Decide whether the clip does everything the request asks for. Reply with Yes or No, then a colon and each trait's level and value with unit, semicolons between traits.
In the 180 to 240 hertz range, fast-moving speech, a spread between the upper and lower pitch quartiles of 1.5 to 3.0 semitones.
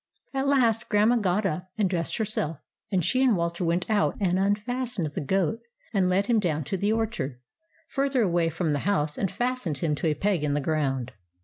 No: high, 190 Hz; fast, 210 wpm; average, 5.3 semitones